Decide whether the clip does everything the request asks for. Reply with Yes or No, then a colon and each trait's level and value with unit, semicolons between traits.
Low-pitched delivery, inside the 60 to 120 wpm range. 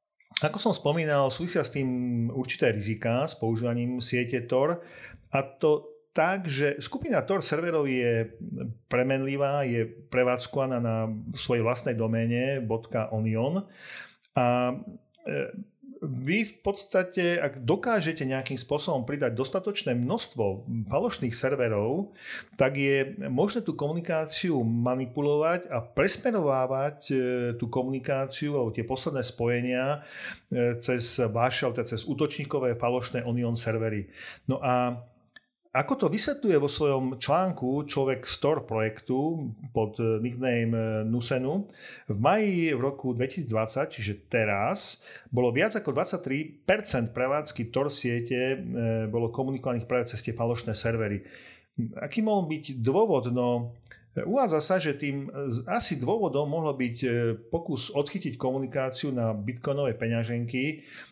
Yes: low, 130 Hz; average, 115 wpm